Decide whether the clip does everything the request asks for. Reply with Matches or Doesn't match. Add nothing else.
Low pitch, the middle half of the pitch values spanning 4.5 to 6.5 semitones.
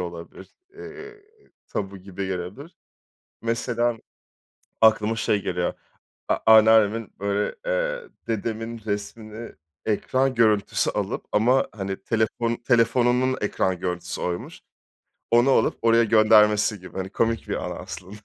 Doesn't match